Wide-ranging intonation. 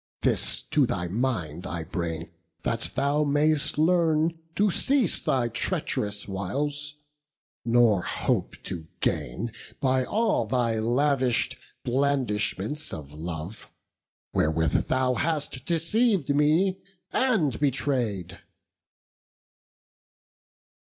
Yes: wide, 6.7 semitones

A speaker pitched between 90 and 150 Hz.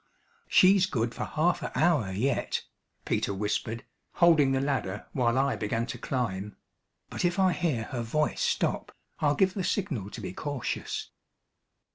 Yes: low, 135 Hz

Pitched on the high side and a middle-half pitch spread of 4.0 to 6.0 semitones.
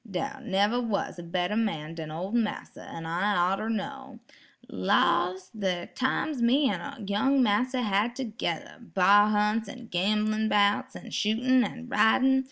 Yes: high, 215 Hz; average, 4.4 semitones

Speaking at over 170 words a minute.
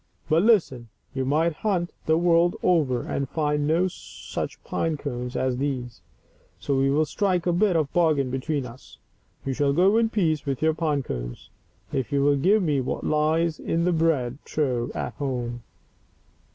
Yes: average, 180 wpm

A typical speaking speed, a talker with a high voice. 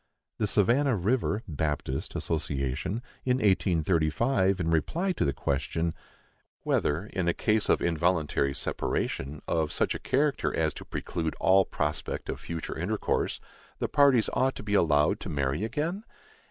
No: average, 145 wpm; very low, 85 Hz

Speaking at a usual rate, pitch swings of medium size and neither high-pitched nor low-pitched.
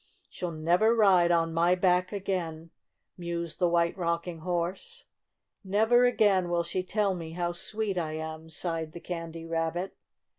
No: average, 150 wpm; narrow, 2.2 semitones; medium, 175 Hz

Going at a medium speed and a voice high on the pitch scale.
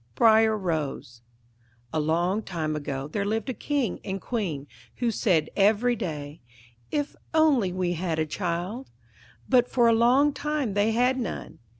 Yes: average, 155 wpm; high, 205 Hz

